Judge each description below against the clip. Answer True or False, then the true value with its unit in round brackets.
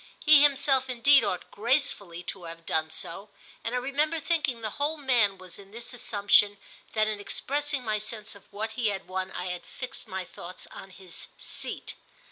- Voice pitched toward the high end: True (215 Hz)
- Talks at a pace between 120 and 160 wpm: False (185 wpm)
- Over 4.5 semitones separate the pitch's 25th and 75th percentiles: True (5.6 semitones)